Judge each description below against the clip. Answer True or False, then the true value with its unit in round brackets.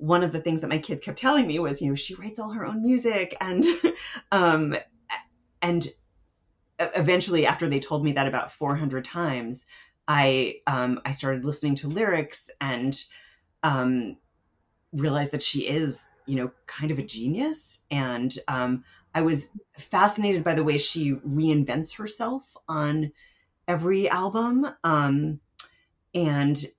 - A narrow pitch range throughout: False (4.7 semitones)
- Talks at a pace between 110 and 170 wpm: True (150 wpm)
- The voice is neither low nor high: True (150 Hz)